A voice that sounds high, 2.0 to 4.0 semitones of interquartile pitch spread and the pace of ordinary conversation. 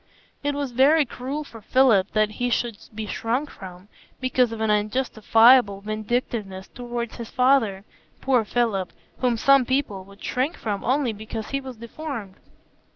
Yes: high, 235 Hz; average, 3.6 semitones; average, 150 wpm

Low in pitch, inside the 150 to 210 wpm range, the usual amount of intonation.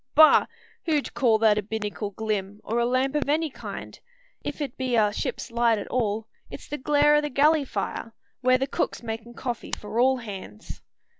No: high, 240 Hz; average, 190 wpm; average, 4.1 semitones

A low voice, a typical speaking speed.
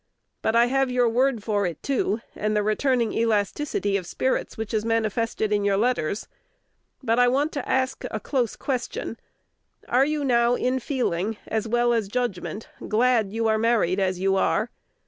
No: high, 230 Hz; average, 175 wpm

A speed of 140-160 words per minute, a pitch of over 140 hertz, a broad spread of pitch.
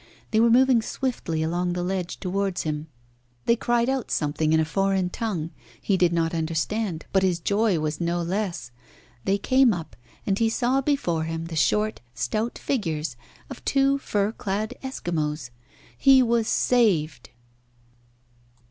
Yes: average, 150 wpm; high, 190 Hz; wide, 5.9 semitones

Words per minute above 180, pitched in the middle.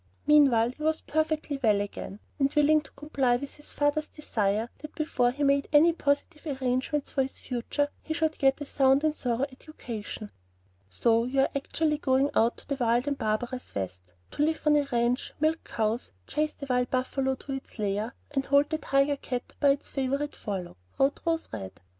No: average, 190 wpm; very high, 275 Hz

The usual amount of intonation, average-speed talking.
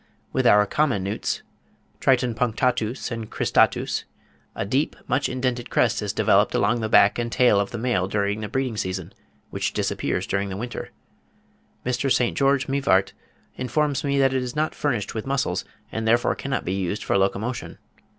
Yes: average, 4.3 semitones; average, 170 wpm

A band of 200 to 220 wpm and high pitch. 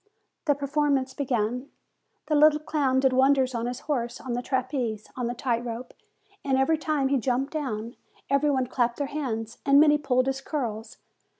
No: average, 185 wpm; very high, 265 Hz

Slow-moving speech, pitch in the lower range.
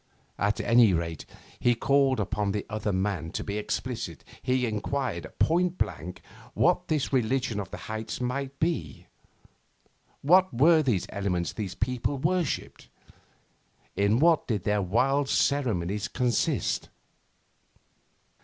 Yes: slow, 125 wpm; low, 115 Hz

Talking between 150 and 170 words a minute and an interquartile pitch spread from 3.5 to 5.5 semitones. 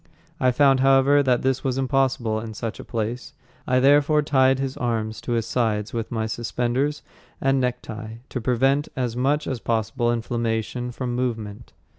No: average, 165 wpm; average, 2.7 semitones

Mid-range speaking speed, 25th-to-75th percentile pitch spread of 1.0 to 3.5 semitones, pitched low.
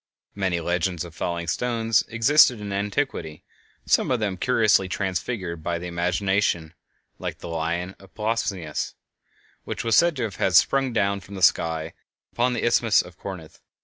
No: average, 160 wpm; average, 4.8 semitones; very low, 95 Hz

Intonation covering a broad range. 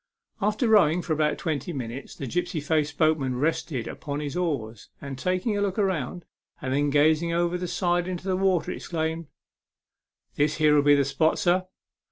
No: average, 3.7 semitones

